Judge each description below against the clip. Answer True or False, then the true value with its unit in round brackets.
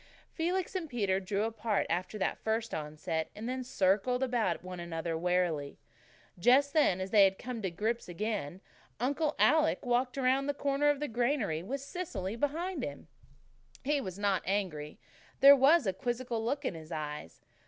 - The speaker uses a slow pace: False (165 wpm)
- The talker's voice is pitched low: False (225 Hz)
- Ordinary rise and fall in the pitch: False (7.1 semitones)